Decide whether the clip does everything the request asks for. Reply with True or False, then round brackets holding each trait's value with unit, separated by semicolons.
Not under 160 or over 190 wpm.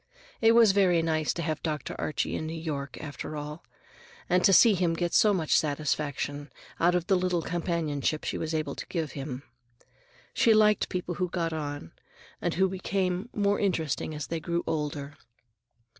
True (175 wpm)